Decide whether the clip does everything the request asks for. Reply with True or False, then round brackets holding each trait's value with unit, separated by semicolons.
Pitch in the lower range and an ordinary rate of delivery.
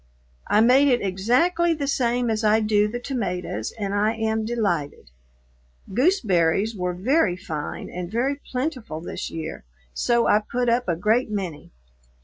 False (220 Hz; 150 wpm)